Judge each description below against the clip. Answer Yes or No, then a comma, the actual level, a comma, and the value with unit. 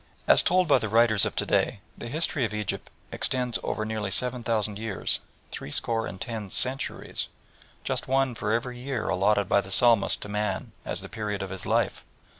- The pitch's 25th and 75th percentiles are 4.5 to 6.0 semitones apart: No, average, 3.2 semitones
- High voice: No, low, 110 Hz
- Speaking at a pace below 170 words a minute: No, average, 195 wpm